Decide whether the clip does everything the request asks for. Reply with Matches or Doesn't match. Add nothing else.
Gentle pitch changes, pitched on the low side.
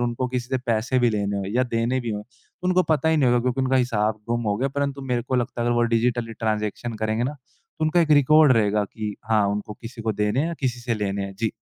Doesn't match